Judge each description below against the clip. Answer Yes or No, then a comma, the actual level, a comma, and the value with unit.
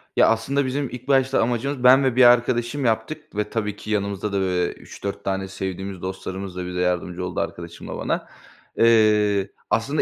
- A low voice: Yes, low, 105 Hz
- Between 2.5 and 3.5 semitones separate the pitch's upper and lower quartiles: No, average, 4.7 semitones